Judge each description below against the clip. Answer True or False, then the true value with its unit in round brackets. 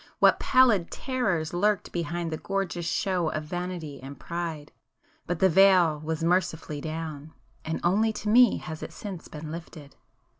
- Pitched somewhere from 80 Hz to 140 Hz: False (170 Hz)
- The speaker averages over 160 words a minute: False (150 wpm)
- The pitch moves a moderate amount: True (3.3 semitones)